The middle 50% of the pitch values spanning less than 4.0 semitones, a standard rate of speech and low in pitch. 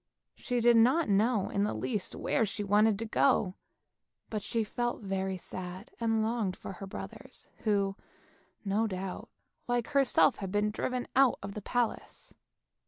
No: average, 3.3 semitones; average, 160 wpm; high, 215 Hz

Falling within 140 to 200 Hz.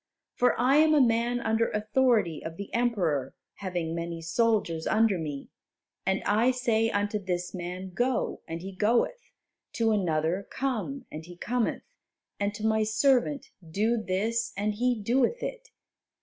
No: high, 215 Hz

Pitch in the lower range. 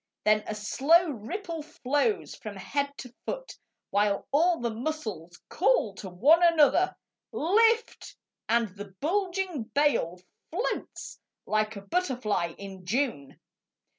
No: very high, 255 Hz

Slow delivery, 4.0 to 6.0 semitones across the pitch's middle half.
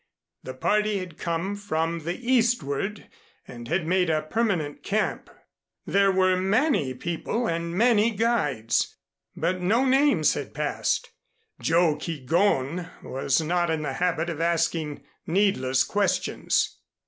Yes: slow, 125 wpm; average, 4.8 semitones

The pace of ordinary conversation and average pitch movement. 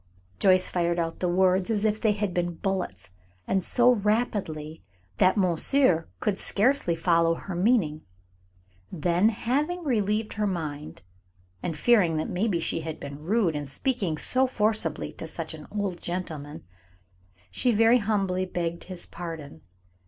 Yes: average, 145 wpm; average, 4.5 semitones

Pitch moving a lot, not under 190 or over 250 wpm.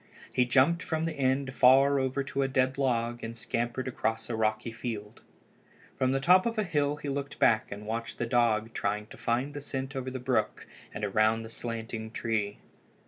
No: average, 3.3 semitones; average, 195 wpm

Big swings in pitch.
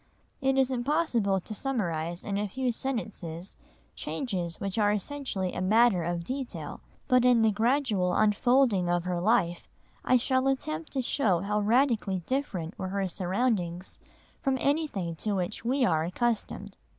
Yes: wide, 6.0 semitones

